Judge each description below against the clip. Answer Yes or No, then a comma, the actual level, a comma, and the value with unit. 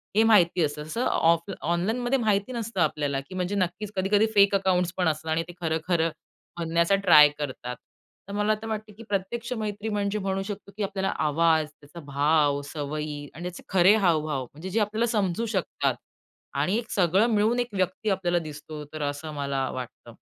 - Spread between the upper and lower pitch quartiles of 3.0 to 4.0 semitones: No, average, 5.1 semitones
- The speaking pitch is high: No, medium, 180 Hz